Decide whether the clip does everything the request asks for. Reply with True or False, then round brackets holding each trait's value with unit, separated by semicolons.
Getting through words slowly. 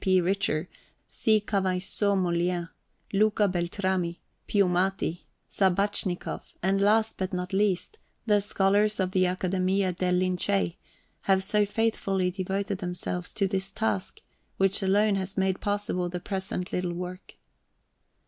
True (125 wpm)